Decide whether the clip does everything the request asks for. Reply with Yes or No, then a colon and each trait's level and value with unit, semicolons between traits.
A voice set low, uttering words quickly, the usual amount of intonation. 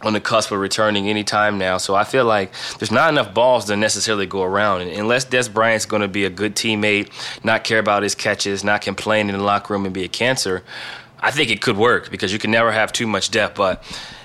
No: low, 105 Hz; fast, 250 wpm; narrow, 1.5 semitones